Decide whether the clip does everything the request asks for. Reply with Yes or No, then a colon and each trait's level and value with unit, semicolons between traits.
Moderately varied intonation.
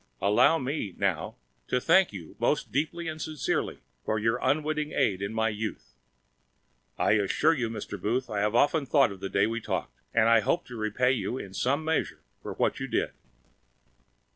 No: wide, 6.0 semitones